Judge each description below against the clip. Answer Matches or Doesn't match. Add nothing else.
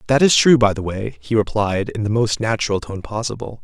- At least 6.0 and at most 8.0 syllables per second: Doesn't match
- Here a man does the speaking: Matches